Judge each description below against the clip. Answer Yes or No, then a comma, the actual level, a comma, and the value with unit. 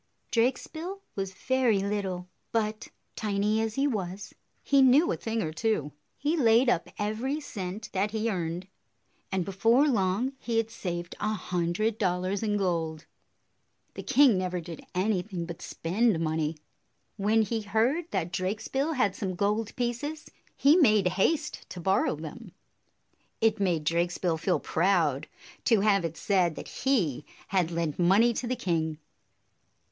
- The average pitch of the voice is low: No, high, 200 Hz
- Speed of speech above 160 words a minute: No, average, 150 wpm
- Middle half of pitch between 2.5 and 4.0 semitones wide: No, average, 4.5 semitones